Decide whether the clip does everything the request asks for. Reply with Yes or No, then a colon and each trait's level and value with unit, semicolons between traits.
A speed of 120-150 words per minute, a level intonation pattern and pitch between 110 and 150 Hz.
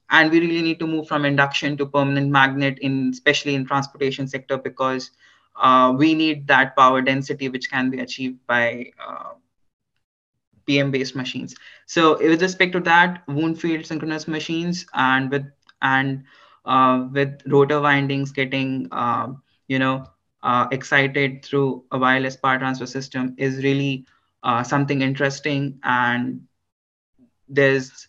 Yes: average, 145 wpm; narrow, 1.6 semitones; low, 135 Hz